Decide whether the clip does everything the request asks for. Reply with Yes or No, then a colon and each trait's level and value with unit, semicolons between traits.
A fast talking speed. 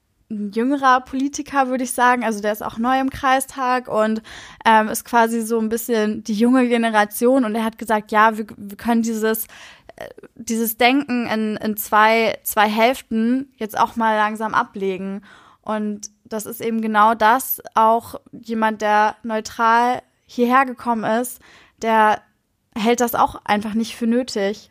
No: average, 160 wpm